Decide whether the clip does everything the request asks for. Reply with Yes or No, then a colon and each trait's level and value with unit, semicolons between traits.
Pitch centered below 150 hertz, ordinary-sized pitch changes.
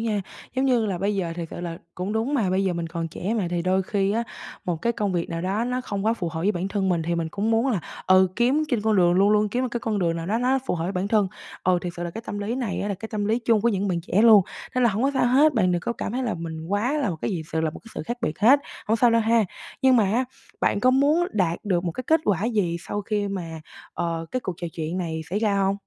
No: high, 200 Hz; average, 4.7 semitones